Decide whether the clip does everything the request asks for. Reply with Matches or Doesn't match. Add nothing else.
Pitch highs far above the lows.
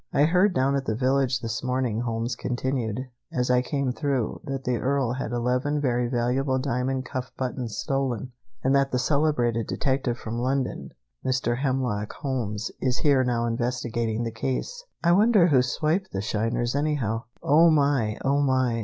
Doesn't match